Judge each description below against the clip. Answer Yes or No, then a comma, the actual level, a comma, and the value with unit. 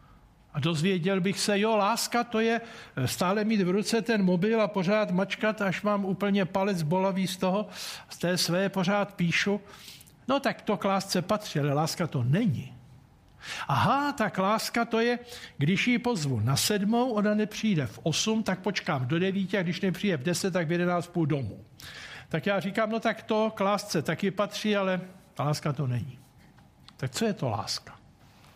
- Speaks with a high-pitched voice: Yes, high, 195 Hz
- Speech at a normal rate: No, fast, 185 wpm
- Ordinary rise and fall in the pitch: Yes, average, 3.6 semitones